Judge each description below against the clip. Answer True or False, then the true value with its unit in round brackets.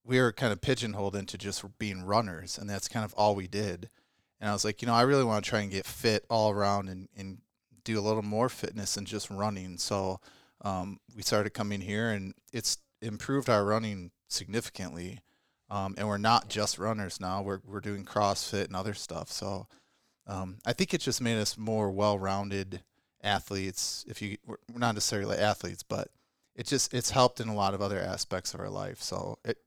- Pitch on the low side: True (105 Hz)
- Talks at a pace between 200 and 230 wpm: True (205 wpm)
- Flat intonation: True (2.2 semitones)